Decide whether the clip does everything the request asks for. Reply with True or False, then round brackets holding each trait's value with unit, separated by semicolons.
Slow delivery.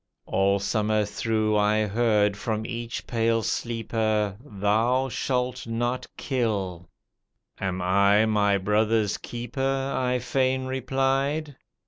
True (105 wpm)